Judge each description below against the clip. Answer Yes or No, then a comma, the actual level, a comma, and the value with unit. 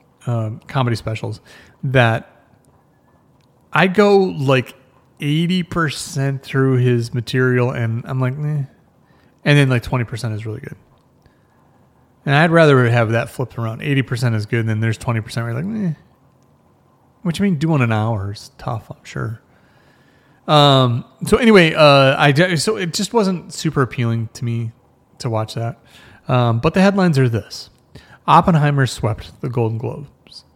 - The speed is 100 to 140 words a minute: No, average, 155 wpm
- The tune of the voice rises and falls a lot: No, average, 4.7 semitones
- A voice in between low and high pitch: No, low, 130 Hz